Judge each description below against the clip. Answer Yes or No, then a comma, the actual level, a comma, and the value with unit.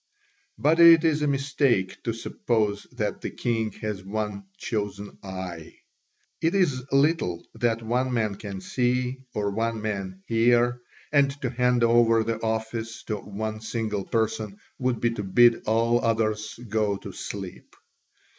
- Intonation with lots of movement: No, average, 2.8 semitones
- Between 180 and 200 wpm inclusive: No, average, 145 wpm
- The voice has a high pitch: No, low, 115 Hz